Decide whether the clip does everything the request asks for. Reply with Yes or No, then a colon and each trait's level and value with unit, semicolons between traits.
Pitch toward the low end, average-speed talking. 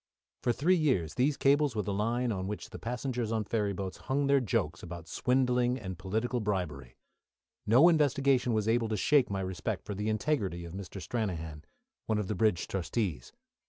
Yes: low, 110 Hz; average, 185 wpm